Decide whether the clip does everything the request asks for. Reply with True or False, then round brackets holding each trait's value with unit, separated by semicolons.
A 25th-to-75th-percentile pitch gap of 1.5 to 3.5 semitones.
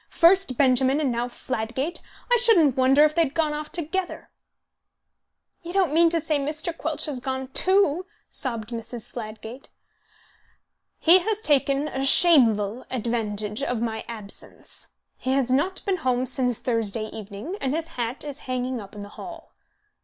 False (5.5 semitones)